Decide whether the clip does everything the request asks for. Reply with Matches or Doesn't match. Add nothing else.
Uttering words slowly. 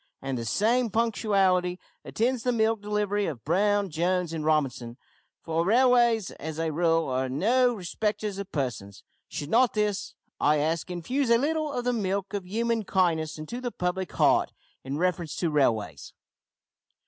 Doesn't match